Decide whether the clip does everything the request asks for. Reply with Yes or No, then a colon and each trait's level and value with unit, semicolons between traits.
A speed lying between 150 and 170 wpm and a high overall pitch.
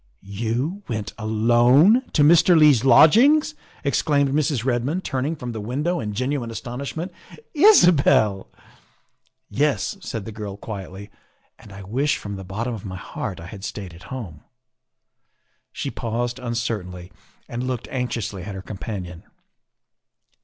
No: average, 165 wpm; low, 120 Hz